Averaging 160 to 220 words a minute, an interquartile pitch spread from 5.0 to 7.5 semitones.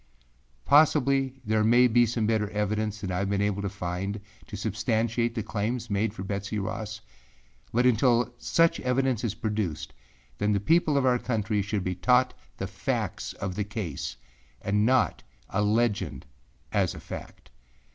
No: average, 165 wpm; average, 3.2 semitones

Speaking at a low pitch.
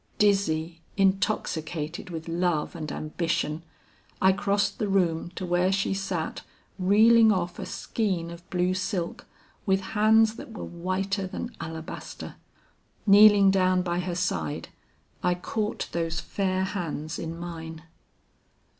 No: medium, 185 Hz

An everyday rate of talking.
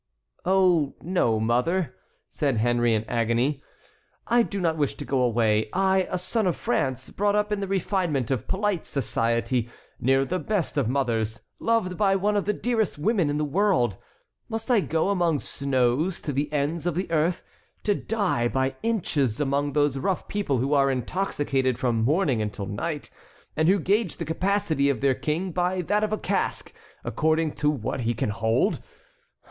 Yes: average, 175 wpm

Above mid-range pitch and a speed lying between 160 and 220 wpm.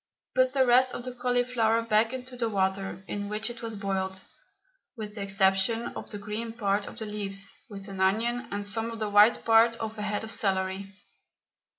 Yes: high, 215 Hz; average, 200 wpm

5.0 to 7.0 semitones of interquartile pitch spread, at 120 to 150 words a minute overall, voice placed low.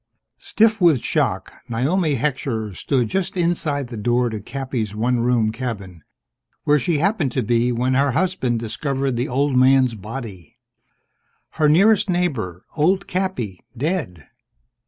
Yes: wide, 5.5 semitones; average, 140 wpm; low, 130 Hz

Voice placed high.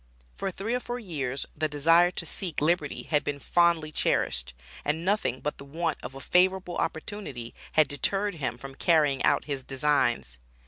No: medium, 155 Hz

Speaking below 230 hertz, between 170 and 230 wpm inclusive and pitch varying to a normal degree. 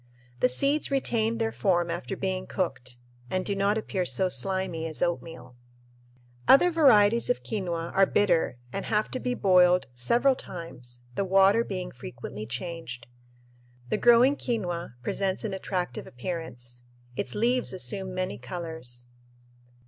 No: medium, 185 Hz; average, 140 wpm; average, 4.5 semitones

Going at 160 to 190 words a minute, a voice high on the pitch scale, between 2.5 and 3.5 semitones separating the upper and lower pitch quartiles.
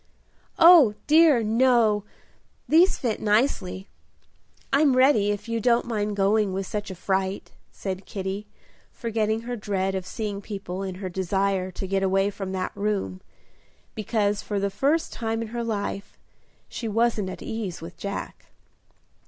No: average, 150 wpm; high, 205 Hz; average, 2.9 semitones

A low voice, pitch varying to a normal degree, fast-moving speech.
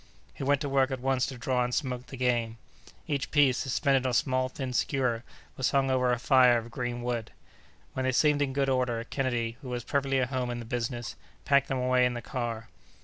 No: low, 130 Hz; narrow, 1.8 semitones; fast, 225 wpm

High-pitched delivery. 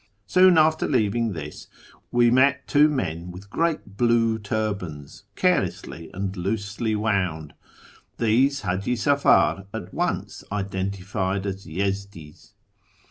No: low, 100 Hz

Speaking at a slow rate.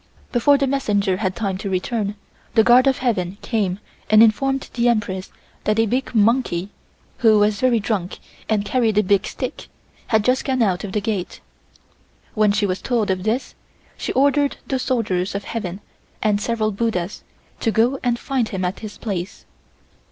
No: average, 175 wpm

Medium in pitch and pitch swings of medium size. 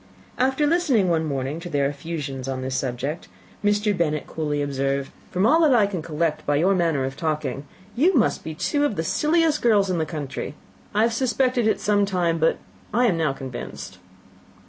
No: medium, 165 Hz; wide, 7.3 semitones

